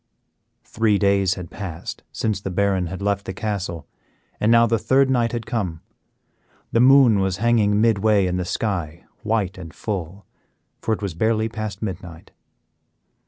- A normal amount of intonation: Yes, average, 3.3 semitones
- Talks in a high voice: No, low, 100 Hz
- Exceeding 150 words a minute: Yes, average, 160 wpm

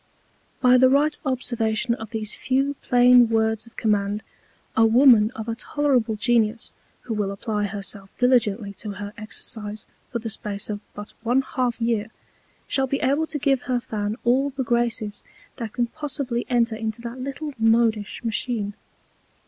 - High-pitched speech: Yes, high, 230 Hz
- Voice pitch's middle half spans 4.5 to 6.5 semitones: No, average, 3.0 semitones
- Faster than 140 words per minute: Yes, average, 160 wpm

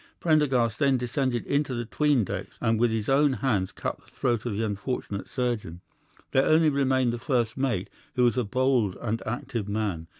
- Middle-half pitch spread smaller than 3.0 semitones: No, average, 3.5 semitones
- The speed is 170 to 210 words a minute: Yes, average, 190 wpm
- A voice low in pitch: Yes, low, 120 Hz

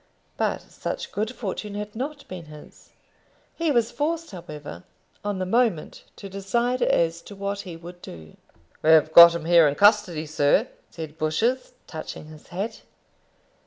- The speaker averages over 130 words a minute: Yes, average, 155 wpm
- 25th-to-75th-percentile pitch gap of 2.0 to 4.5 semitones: No, wide, 5.6 semitones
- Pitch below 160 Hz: No, medium, 185 Hz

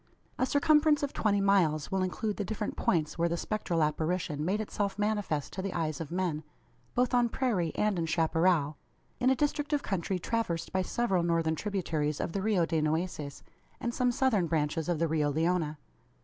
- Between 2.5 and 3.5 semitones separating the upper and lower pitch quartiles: No, average, 4.9 semitones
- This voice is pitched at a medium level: Yes, medium, 180 Hz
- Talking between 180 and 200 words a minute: Yes, average, 190 wpm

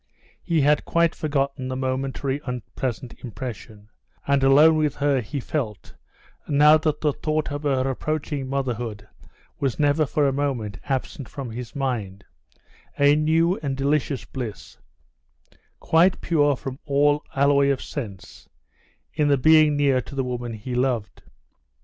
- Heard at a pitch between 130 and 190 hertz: Yes, medium, 140 Hz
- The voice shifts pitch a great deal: No, average, 2.8 semitones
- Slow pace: No, average, 145 wpm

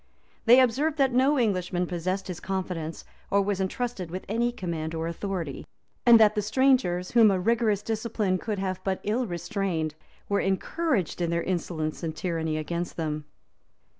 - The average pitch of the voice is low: No, high, 190 Hz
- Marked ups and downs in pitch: No, average, 4.7 semitones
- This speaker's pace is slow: No, average, 165 wpm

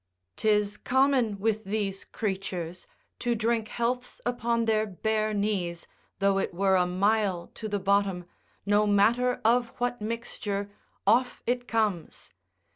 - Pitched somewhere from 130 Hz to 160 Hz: No, high, 210 Hz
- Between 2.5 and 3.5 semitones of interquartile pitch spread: Yes, average, 2.8 semitones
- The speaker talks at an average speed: No, slow, 130 wpm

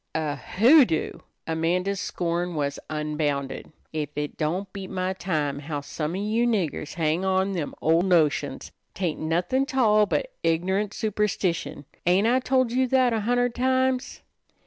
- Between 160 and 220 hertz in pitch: Yes, medium, 185 Hz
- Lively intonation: Yes, wide, 6.0 semitones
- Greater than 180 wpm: No, average, 155 wpm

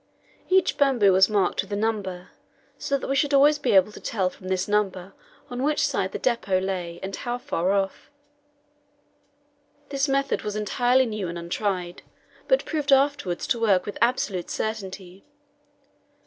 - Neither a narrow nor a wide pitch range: No, wide, 5.8 semitones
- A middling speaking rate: Yes, average, 160 wpm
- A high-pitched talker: Yes, high, 210 Hz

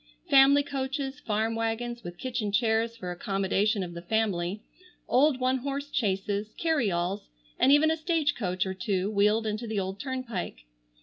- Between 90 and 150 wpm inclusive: No, average, 160 wpm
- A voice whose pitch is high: Yes, high, 225 Hz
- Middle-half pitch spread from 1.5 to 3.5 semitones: No, average, 5.2 semitones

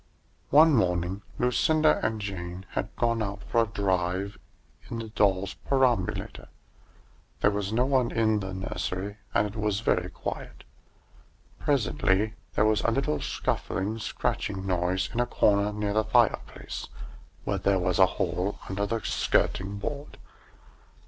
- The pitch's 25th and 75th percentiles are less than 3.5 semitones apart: Yes, average, 3.1 semitones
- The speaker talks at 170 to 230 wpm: No, average, 140 wpm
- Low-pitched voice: Yes, low, 105 Hz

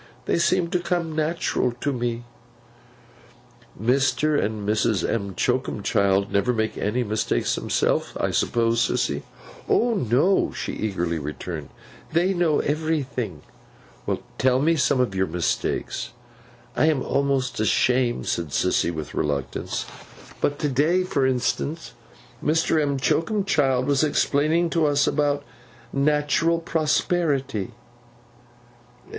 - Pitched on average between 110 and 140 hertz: Yes, low, 135 Hz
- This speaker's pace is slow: Yes, slow, 115 wpm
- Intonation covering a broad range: Yes, wide, 6.2 semitones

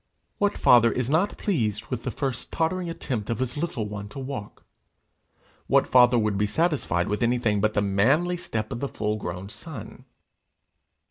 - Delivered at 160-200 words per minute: Yes, average, 175 wpm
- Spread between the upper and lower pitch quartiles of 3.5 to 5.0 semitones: No, wide, 5.4 semitones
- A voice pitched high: No, low, 120 Hz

